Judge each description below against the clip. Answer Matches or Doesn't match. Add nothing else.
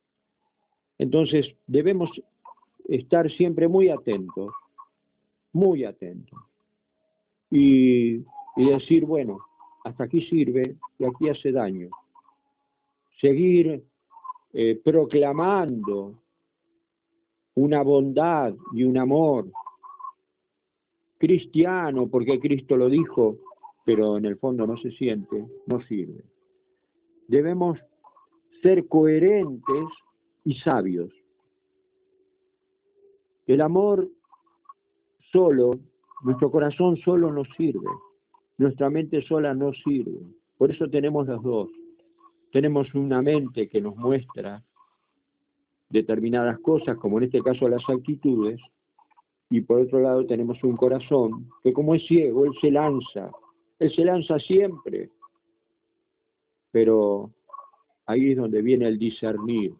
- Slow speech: Matches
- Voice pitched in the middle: Matches